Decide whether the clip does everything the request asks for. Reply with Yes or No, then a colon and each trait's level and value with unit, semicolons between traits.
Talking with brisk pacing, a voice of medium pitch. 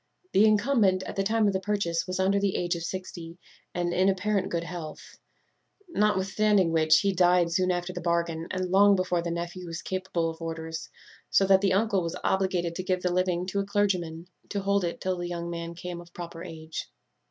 Yes: fast, 210 wpm; medium, 180 Hz